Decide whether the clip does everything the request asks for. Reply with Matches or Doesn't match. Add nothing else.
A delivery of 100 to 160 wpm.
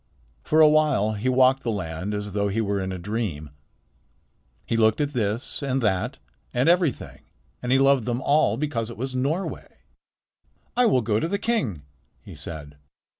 Doesn't match